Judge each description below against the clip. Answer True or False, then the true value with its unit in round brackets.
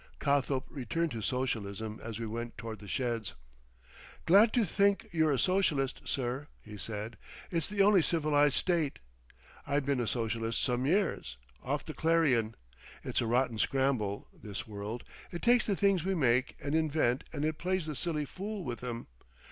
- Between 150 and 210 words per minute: True (165 wpm)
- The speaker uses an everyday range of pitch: False (6.3 semitones)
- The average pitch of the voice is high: False (135 Hz)